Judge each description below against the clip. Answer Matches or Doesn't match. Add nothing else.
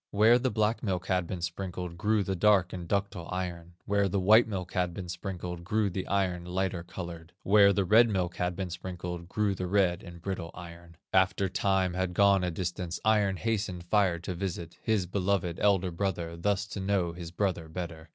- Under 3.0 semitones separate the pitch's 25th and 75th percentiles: Matches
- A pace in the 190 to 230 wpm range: Matches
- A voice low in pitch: Matches